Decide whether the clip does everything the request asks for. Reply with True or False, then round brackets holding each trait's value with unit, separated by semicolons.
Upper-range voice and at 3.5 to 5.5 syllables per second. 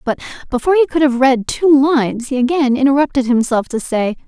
False (265 Hz; 5.8 syllables/s)